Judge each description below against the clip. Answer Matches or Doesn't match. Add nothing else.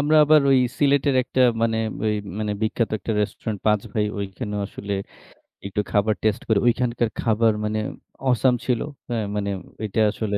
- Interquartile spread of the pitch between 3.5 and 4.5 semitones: Doesn't match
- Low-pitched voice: Matches